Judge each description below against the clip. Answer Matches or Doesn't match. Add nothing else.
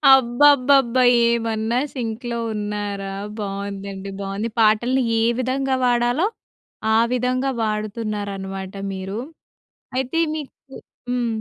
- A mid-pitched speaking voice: Doesn't match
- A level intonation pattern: Doesn't match